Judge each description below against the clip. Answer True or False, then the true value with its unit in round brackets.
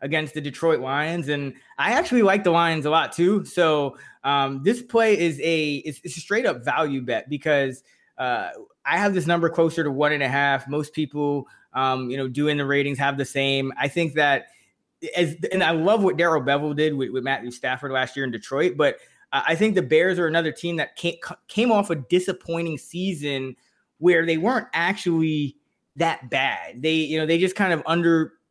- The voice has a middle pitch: True (155 Hz)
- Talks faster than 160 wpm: True (205 wpm)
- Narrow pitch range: False (3.4 semitones)